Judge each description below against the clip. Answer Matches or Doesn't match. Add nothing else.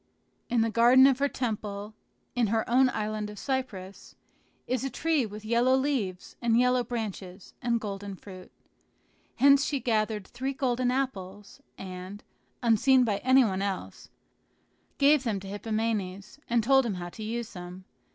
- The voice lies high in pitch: Matches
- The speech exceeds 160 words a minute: Doesn't match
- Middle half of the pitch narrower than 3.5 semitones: Doesn't match